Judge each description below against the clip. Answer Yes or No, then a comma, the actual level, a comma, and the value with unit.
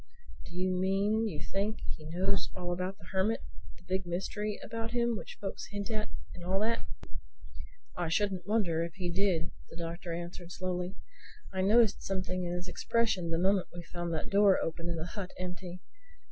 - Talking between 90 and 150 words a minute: No, average, 185 wpm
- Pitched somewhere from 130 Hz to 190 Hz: Yes, medium, 185 Hz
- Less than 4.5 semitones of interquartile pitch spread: Yes, narrow, 2.6 semitones